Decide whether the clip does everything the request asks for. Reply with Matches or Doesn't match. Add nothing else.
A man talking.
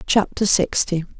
Doesn't match